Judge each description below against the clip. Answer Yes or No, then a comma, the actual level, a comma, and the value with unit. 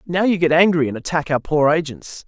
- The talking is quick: Yes, fast, 235 wpm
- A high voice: No, medium, 160 Hz